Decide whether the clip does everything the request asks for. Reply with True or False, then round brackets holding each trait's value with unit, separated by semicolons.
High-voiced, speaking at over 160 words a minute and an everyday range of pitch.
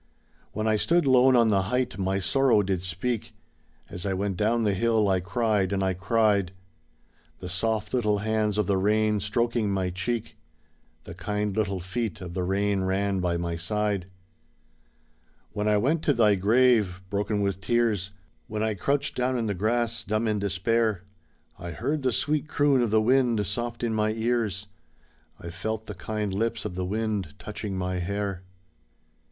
False (105 Hz; 175 wpm; 3.2 semitones)